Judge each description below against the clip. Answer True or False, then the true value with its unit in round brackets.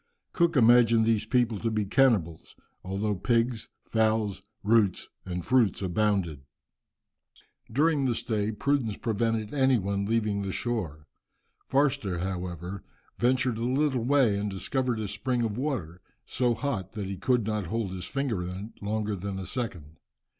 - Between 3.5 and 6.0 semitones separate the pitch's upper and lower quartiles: True (4.1 semitones)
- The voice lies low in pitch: True (110 Hz)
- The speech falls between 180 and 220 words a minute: False (150 wpm)